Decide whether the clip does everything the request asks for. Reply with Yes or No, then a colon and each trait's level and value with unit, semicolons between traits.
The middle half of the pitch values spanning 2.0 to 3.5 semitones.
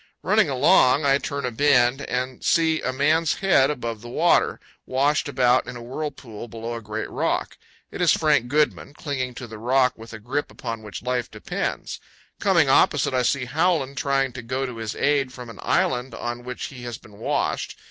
Yes: average, 3.0 semitones